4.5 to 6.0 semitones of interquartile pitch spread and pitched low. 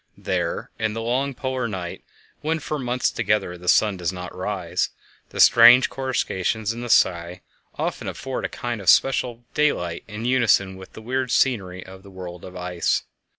Yes: wide, 5.5 semitones; low, 105 Hz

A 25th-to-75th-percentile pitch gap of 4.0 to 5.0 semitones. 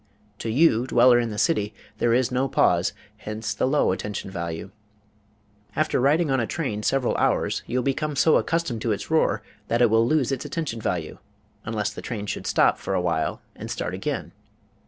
Yes: average, 4.5 semitones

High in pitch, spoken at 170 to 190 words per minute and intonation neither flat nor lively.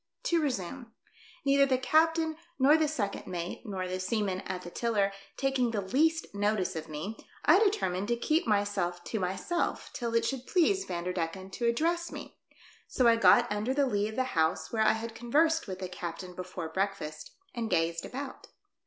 No: high, 220 Hz; average, 180 wpm; wide, 6.7 semitones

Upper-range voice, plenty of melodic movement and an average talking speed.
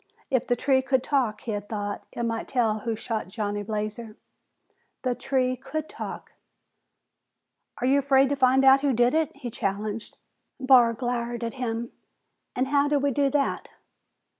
No: high, 245 Hz; average, 3.2 semitones; average, 165 wpm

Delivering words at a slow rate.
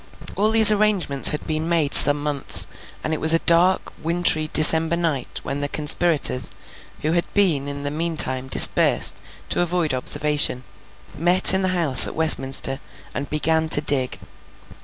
No: average, 160 wpm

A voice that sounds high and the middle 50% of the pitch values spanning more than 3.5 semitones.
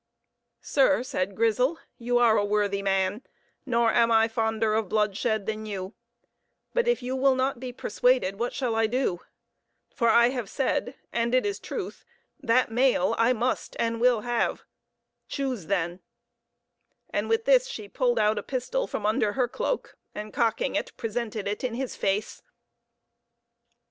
No: high, 230 Hz; average, 3.2 semitones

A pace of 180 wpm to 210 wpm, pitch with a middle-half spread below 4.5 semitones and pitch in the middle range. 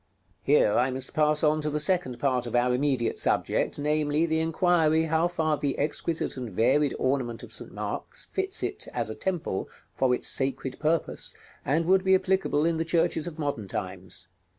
Yes: average, 185 wpm; average, 3.9 semitones; medium, 150 Hz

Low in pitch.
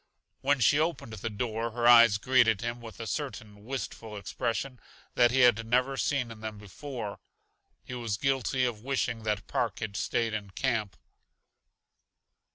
Yes: low, 115 Hz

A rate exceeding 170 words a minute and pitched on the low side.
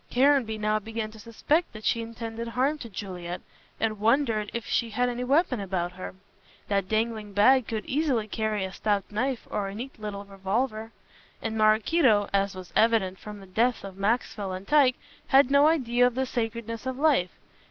No: average, 185 wpm; high, 225 Hz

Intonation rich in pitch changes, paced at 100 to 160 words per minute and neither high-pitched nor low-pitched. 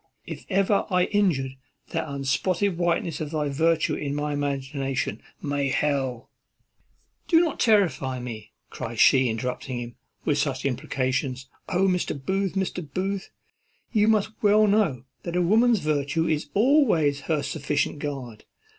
Yes: wide, 6.0 semitones; average, 145 wpm; medium, 150 Hz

